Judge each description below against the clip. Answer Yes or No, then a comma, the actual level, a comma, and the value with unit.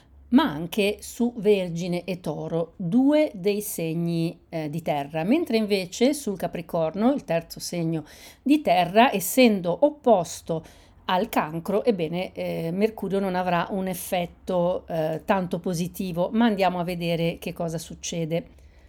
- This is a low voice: No, medium, 180 Hz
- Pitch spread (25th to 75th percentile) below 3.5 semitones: No, average, 4.0 semitones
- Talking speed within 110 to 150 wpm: Yes, average, 135 wpm